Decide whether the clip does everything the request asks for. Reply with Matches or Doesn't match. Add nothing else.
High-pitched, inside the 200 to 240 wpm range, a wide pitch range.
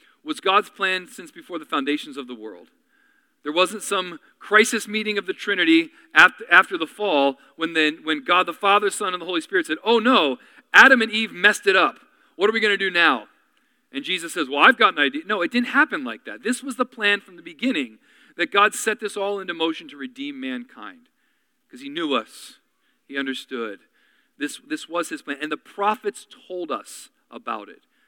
Matches